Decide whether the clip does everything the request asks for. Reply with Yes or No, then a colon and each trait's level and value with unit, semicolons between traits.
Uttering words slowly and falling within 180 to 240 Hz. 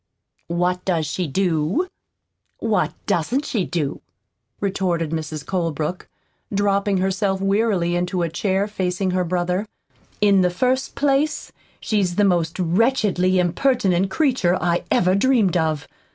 Yes: slow, 125 wpm; medium, 185 Hz